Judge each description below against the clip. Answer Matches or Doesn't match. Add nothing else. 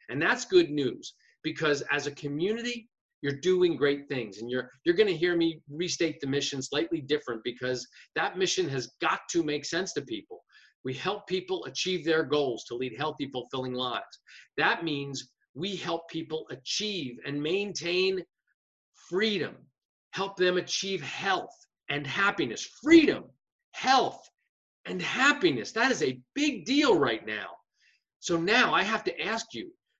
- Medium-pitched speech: Matches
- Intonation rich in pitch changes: Matches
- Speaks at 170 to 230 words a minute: Doesn't match